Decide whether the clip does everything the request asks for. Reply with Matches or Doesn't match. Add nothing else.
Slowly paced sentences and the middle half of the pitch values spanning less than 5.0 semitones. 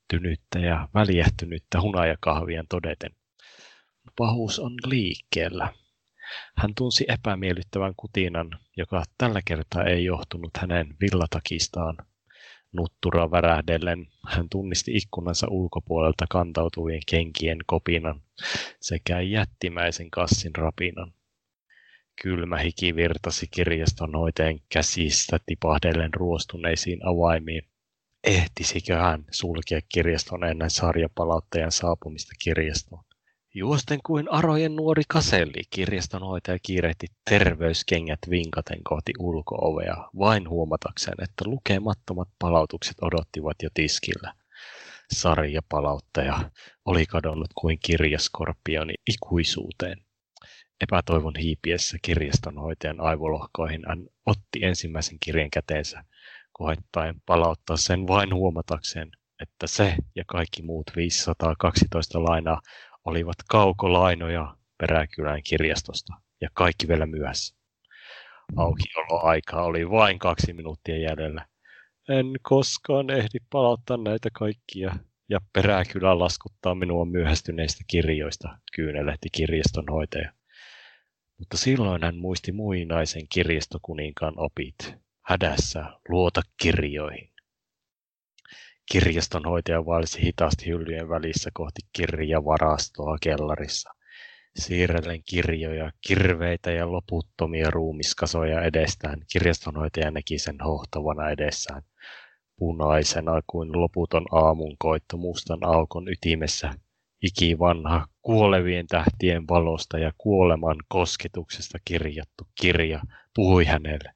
Matches